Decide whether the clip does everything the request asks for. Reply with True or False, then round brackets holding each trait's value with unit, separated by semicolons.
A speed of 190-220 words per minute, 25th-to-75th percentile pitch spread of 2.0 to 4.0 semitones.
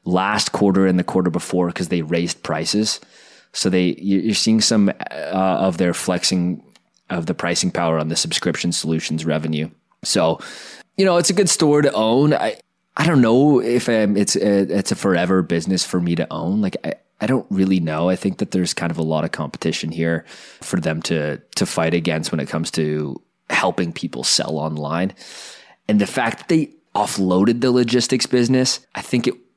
False (195 wpm; 4.8 semitones)